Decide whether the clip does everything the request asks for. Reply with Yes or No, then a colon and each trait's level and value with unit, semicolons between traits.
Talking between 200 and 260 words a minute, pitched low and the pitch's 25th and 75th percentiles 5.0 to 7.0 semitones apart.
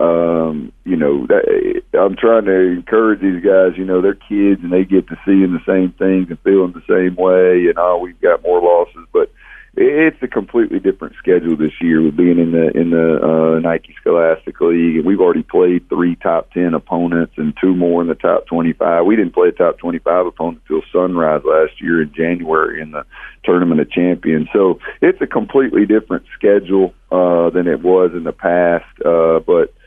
No: fast, 205 wpm; very low, 90 Hz; average, 4.2 semitones